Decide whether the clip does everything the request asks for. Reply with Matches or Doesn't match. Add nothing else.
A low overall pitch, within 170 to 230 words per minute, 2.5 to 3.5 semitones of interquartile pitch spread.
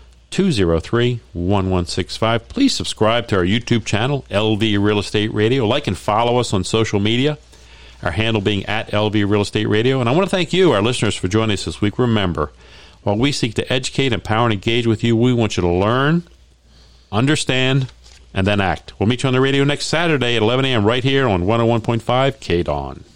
Doesn't match